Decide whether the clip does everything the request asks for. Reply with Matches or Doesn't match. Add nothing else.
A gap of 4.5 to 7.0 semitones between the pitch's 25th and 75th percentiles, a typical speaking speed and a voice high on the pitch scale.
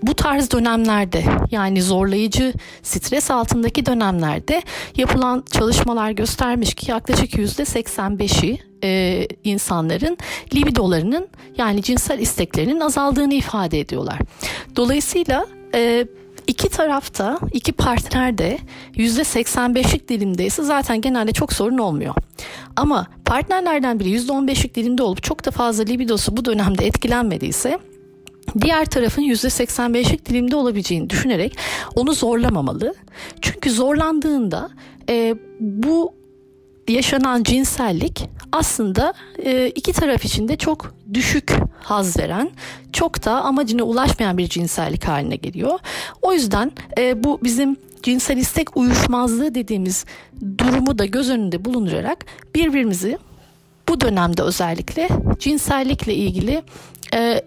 Matches